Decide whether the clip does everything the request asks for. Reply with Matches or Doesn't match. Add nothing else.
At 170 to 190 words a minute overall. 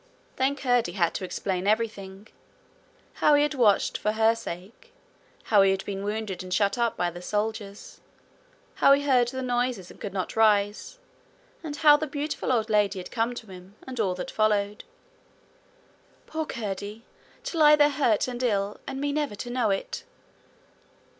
Matches